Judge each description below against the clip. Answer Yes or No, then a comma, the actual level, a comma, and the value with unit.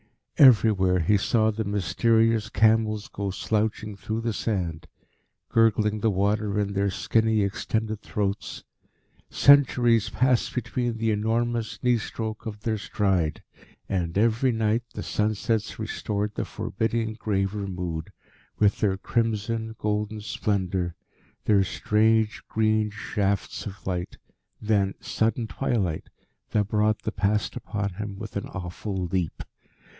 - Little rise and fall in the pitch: Yes, narrow, 2.1 semitones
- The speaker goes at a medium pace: No, slow, 125 wpm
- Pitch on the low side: Yes, low, 105 Hz